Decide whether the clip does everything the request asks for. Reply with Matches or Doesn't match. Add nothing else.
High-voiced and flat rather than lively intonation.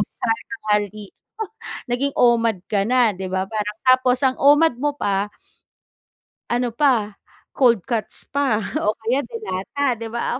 Doesn't match